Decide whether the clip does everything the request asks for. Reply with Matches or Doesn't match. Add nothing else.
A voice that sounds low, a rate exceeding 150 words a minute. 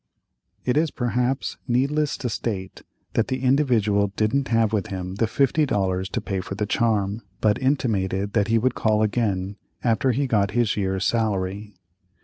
Matches